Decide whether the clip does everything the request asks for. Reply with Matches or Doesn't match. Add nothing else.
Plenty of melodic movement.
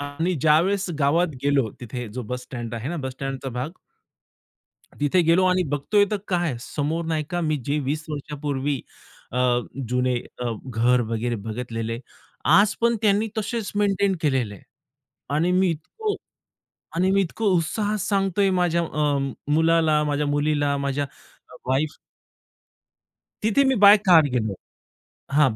Matches